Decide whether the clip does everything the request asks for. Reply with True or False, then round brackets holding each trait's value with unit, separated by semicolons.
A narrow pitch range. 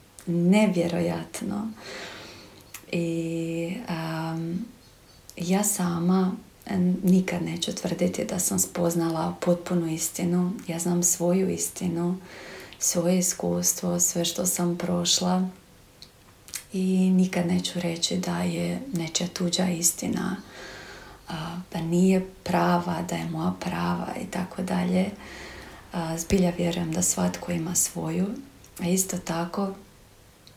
True (1.5 semitones)